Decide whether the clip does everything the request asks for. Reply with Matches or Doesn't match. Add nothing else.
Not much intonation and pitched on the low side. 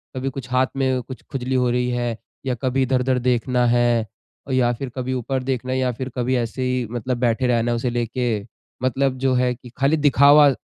Matches